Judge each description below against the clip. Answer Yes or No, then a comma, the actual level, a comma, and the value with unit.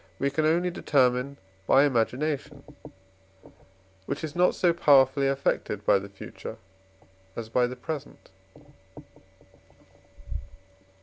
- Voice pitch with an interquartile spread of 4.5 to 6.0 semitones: No, average, 3.4 semitones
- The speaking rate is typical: No, slow, 105 wpm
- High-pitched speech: No, medium, 140 Hz